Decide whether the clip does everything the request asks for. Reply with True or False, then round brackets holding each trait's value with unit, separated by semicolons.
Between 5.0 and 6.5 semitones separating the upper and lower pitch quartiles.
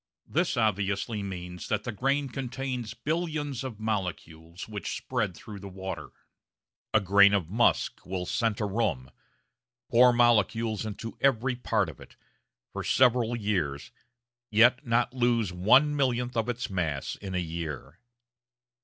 False (4.5 semitones)